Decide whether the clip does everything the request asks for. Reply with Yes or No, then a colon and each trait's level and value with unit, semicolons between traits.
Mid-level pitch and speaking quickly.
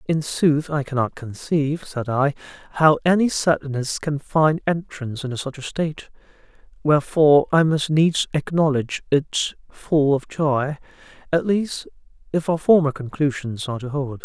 No: medium, 145 Hz; average, 145 wpm